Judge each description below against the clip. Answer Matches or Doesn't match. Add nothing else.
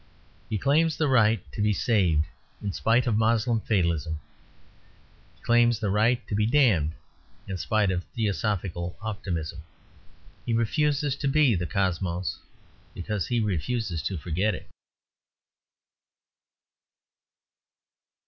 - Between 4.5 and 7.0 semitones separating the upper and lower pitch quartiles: Matches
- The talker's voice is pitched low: Matches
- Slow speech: Matches